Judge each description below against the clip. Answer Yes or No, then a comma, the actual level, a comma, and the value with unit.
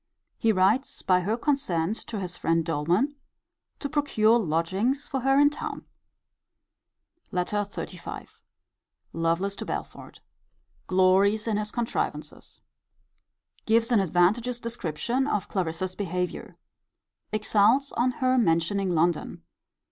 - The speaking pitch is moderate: No, high, 205 Hz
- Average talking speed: No, slow, 110 wpm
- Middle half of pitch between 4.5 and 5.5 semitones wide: Yes, average, 5.0 semitones